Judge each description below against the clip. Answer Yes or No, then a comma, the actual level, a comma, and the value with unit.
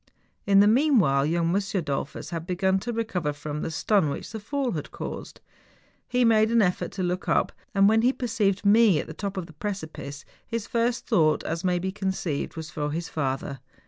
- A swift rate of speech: Yes, fast, 210 wpm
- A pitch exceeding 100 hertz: Yes, high, 190 Hz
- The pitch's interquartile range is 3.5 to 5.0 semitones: No, wide, 5.4 semitones